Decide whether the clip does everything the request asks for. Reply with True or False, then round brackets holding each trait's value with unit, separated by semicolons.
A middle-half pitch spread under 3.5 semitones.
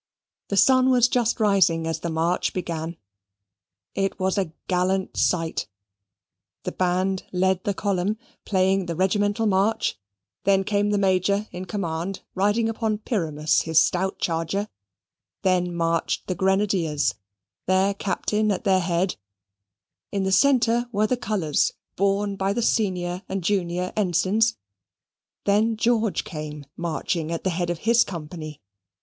True (3.0 semitones)